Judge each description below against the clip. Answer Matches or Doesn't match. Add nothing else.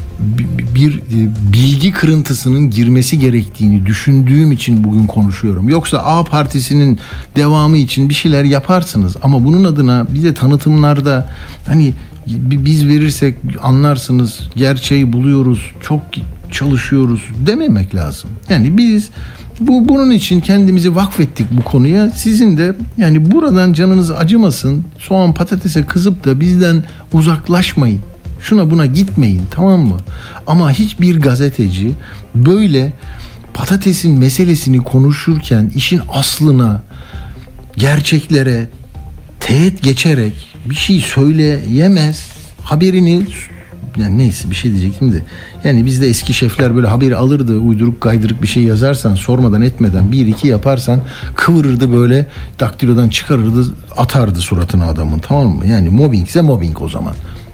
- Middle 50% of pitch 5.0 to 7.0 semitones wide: Matches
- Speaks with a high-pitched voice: Doesn't match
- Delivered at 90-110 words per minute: Doesn't match